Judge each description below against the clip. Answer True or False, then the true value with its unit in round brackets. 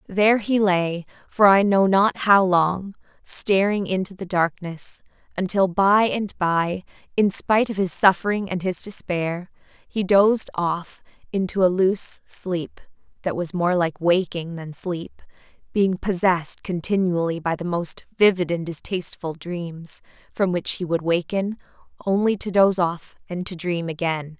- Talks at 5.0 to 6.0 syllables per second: False (4.3 syllables/s)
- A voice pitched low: False (185 Hz)